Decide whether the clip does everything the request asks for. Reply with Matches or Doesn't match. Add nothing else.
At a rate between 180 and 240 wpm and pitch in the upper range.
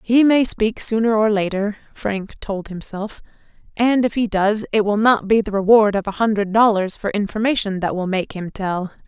Matches